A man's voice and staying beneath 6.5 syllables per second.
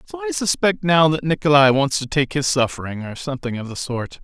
Yes: male; 5.7 syllables/s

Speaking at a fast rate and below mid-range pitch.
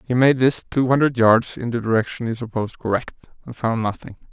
Yes: fast, 210 wpm; low, 120 Hz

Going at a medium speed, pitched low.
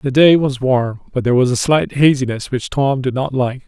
No: fast, 245 wpm; low, 130 Hz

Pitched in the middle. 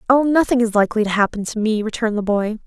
No: high, 220 Hz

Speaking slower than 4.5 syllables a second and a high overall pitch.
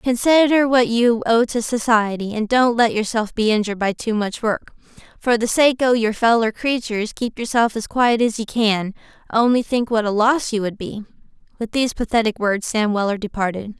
No: 5.1 syllables/s; high, 225 Hz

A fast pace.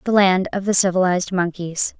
No: average, 180 wpm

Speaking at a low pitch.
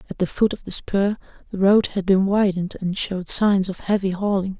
No: high, 195 Hz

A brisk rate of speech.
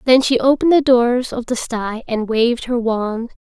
Yes: fast, 210 wpm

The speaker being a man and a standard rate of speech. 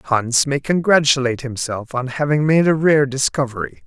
Yes: male; average, 155 wpm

